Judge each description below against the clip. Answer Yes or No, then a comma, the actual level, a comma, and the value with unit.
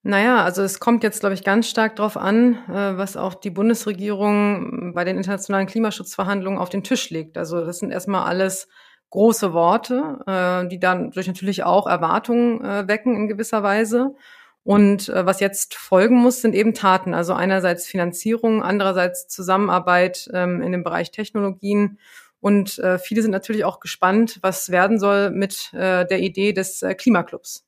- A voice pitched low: No, high, 200 Hz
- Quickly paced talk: No, average, 155 wpm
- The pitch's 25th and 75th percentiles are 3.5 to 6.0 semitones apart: No, average, 2.9 semitones